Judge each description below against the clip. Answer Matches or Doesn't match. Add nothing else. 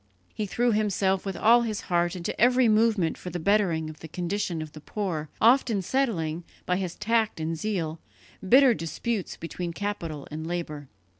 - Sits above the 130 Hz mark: Matches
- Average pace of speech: Matches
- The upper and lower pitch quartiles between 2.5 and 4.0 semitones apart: Doesn't match